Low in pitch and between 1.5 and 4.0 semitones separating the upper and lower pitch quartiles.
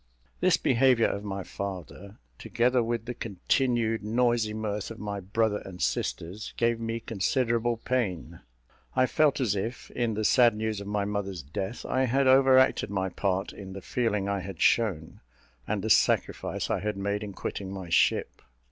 Yes: low, 105 Hz; average, 3.3 semitones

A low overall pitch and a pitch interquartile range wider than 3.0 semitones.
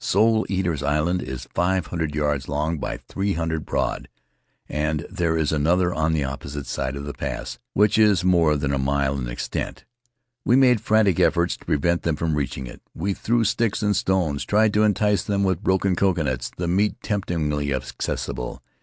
Yes: very low, 85 Hz; average, 5.2 semitones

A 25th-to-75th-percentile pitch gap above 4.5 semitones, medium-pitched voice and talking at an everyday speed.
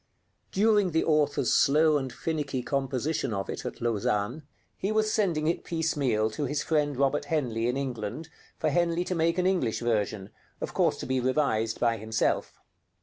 Yes: wide, 5.5 semitones; medium, 145 Hz; average, 170 wpm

